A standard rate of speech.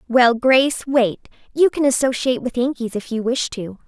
Yes: average, 185 wpm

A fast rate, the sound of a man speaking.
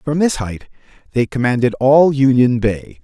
No: average, 160 wpm; male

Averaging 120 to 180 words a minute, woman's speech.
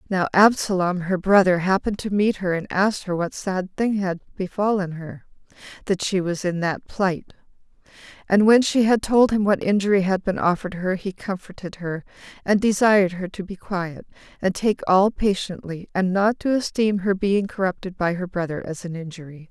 No: average, 190 wpm; female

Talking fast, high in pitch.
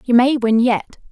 Yes: fast, 215 wpm; high, 240 Hz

